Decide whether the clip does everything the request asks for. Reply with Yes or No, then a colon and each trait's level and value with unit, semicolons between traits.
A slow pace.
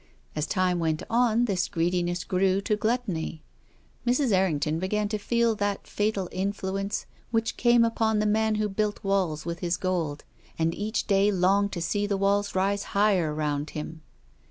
No: average, 170 wpm